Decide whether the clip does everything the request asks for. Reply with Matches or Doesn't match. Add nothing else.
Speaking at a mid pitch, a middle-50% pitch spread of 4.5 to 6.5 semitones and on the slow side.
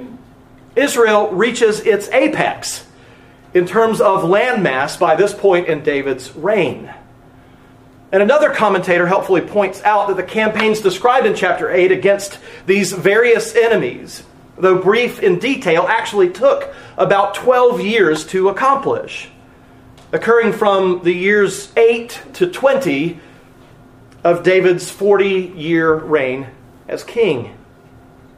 Doesn't match